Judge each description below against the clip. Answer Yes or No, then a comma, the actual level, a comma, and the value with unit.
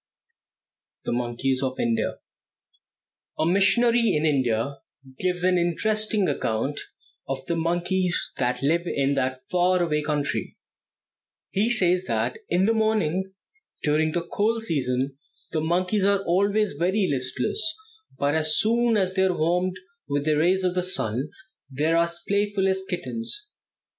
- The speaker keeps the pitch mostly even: No, average, 5.2 semitones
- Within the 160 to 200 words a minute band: No, average, 145 wpm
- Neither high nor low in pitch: Yes, medium, 175 Hz